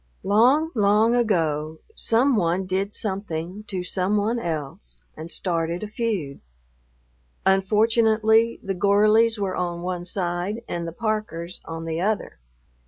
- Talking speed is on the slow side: Yes, slow, 130 wpm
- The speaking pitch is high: Yes, high, 195 Hz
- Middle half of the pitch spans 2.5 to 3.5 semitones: No, average, 4.1 semitones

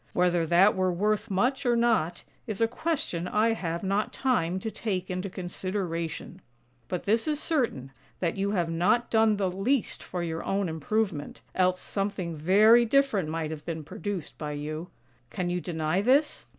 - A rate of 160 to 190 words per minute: Yes, average, 170 wpm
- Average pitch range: Yes, average, 4.6 semitones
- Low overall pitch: No, medium, 185 Hz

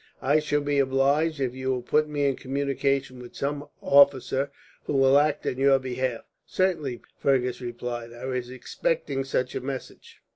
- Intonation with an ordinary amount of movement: No, narrow, 1.8 semitones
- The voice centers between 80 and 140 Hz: Yes, low, 135 Hz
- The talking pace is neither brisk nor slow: Yes, average, 170 wpm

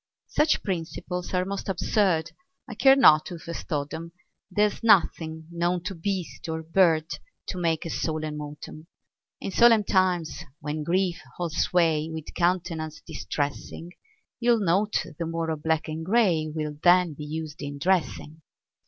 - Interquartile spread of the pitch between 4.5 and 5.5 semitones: No, average, 2.9 semitones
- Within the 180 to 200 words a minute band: No, average, 155 wpm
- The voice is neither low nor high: Yes, medium, 165 Hz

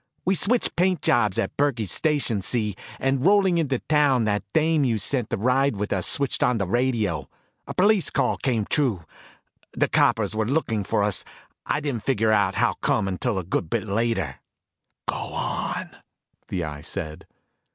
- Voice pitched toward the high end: No, low, 115 Hz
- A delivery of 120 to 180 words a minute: Yes, average, 170 wpm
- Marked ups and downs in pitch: Yes, wide, 6.0 semitones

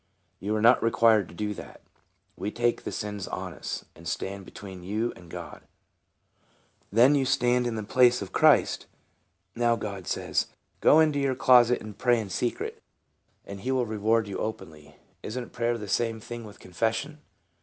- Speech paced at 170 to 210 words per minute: Yes, average, 180 wpm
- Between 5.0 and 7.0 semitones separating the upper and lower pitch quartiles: No, average, 3.2 semitones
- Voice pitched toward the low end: Yes, low, 115 Hz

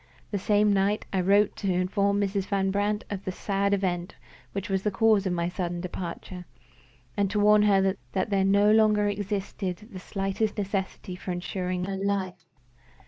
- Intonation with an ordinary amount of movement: No, narrow, 1.6 semitones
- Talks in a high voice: Yes, high, 195 Hz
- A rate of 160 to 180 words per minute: Yes, average, 175 wpm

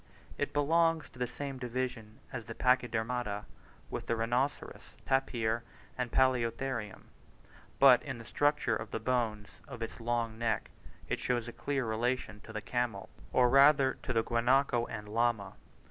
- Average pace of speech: Yes, average, 155 wpm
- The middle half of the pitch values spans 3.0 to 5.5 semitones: No, narrow, 2.6 semitones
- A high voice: No, low, 120 Hz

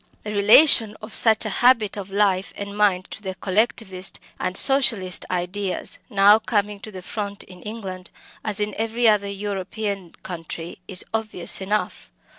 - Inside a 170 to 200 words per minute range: No, average, 155 wpm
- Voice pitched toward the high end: Yes, high, 205 Hz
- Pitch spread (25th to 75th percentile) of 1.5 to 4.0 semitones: Yes, narrow, 2.4 semitones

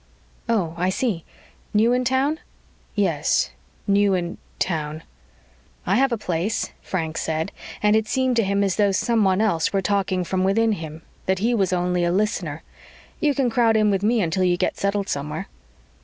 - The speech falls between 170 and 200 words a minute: Yes, average, 175 wpm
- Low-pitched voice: No, high, 195 Hz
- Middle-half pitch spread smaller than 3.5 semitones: No, average, 3.9 semitones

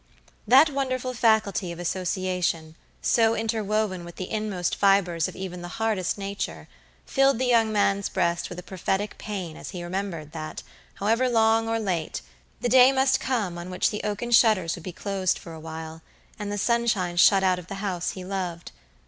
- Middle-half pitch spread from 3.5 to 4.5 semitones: Yes, average, 4.1 semitones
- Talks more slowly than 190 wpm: Yes, average, 180 wpm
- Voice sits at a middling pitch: No, high, 195 Hz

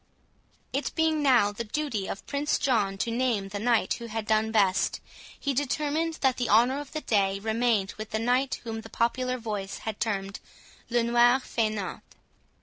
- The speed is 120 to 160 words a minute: No, average, 175 wpm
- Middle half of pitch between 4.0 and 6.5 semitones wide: No, average, 3.4 semitones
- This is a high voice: Yes, high, 230 Hz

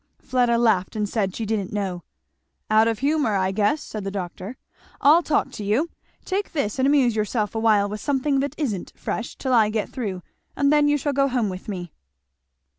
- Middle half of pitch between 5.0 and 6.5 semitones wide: Yes, average, 5.3 semitones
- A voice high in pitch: Yes, high, 225 Hz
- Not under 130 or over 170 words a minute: No, average, 195 wpm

